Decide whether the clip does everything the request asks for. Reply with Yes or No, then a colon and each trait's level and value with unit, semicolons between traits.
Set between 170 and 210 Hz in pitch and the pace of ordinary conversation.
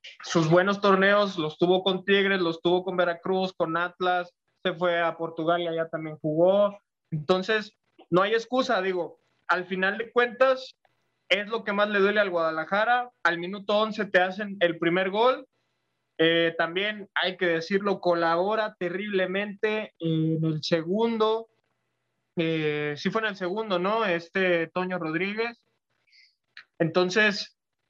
Yes: medium, 185 Hz; average, 145 wpm